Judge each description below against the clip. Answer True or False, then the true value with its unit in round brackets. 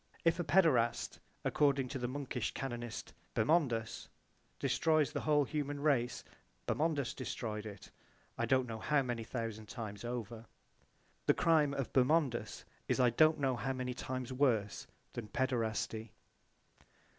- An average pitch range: True (3.8 semitones)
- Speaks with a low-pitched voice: True (130 Hz)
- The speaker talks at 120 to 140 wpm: True (135 wpm)